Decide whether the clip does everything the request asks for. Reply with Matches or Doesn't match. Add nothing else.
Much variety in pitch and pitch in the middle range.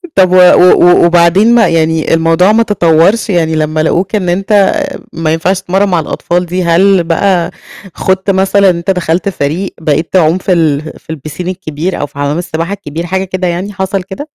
Doesn't match